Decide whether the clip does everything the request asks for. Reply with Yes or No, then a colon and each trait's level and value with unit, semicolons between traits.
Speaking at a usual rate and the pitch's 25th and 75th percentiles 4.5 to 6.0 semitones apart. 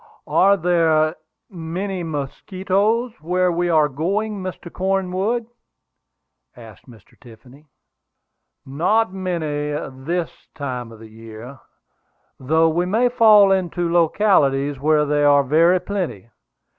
No: slow, 115 wpm; average, 4.9 semitones